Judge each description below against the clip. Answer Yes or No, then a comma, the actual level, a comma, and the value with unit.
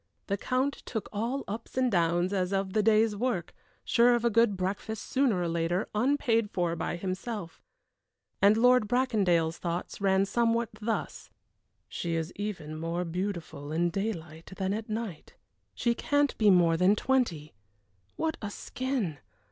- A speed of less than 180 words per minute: Yes, average, 155 wpm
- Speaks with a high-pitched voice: Yes, high, 200 Hz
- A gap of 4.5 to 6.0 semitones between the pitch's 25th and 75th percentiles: Yes, average, 5.0 semitones